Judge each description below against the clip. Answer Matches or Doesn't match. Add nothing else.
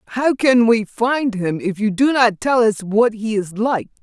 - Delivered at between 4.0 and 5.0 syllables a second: Matches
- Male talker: Doesn't match